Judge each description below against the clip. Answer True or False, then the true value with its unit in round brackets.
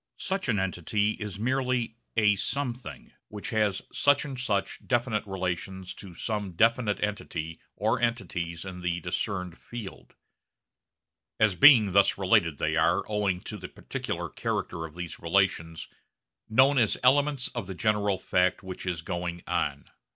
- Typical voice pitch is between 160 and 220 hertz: False (100 Hz)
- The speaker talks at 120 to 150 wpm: True (145 wpm)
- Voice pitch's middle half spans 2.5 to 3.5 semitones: False (4.6 semitones)